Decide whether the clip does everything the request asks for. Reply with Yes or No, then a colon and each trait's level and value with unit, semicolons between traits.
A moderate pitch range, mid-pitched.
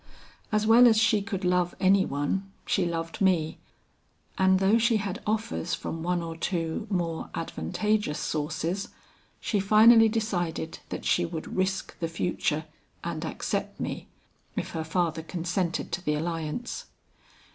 Yes: average, 4.1 semitones; medium, 180 Hz